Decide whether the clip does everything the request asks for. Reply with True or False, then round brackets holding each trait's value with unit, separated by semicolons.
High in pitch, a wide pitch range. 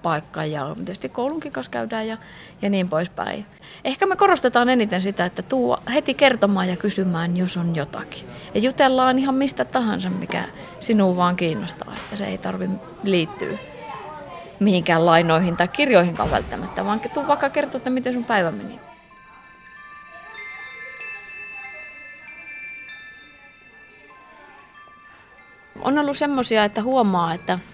True (200 Hz; 7.8 semitones)